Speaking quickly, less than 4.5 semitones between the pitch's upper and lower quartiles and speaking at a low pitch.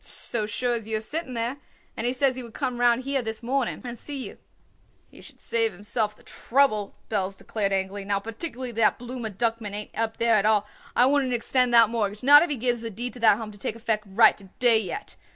No: fast, 235 wpm; average, 2.8 semitones; high, 230 Hz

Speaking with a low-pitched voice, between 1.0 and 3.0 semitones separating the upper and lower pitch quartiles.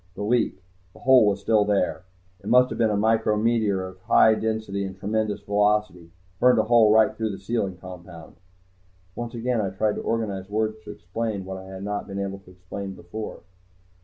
Yes: low, 105 Hz; narrow, 2.6 semitones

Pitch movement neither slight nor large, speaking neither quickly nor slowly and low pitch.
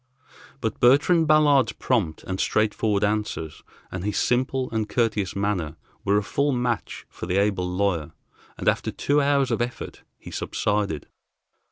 Yes: average, 4.5 semitones; average, 150 wpm; low, 105 Hz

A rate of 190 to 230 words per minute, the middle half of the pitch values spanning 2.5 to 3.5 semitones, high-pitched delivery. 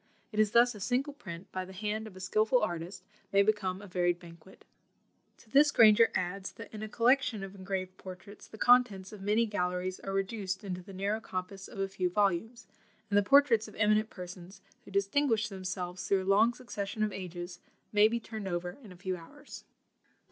Yes: average, 200 wpm; average, 2.8 semitones; high, 200 Hz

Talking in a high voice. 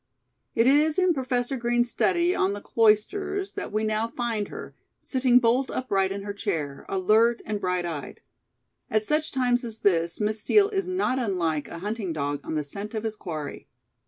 Yes: high, 220 Hz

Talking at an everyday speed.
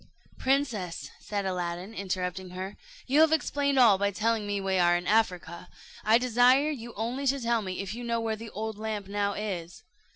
Yes: average, 190 wpm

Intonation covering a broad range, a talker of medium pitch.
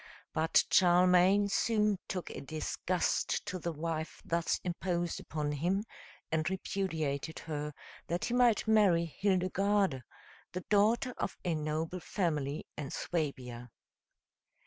No: average, 3.6 semitones; medium, 175 Hz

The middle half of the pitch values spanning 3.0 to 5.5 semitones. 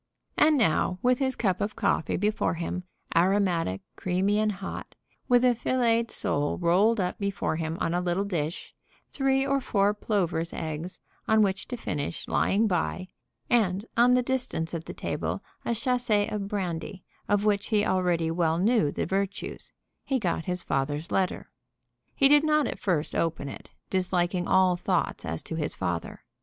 Yes: average, 4.7 semitones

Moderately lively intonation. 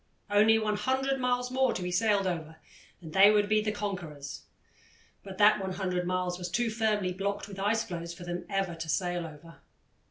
Yes: average, 3.3 semitones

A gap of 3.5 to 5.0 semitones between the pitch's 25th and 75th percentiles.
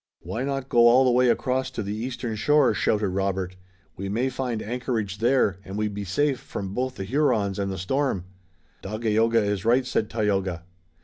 Yes: average, 4.4 semitones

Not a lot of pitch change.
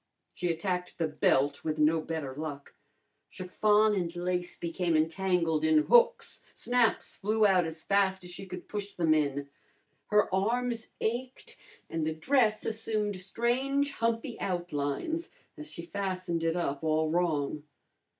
No: average, 5.1 semitones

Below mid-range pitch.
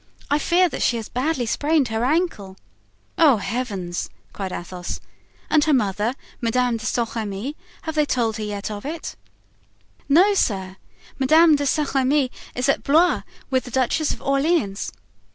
No: very high, 255 Hz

